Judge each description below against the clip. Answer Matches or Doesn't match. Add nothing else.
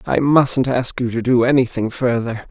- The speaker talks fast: Doesn't match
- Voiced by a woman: Doesn't match